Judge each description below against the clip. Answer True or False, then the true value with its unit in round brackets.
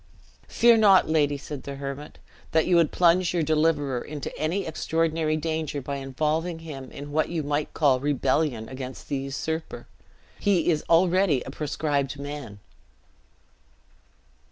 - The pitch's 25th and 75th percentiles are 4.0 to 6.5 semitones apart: False (2.8 semitones)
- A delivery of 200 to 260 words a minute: False (140 wpm)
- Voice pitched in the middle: True (150 Hz)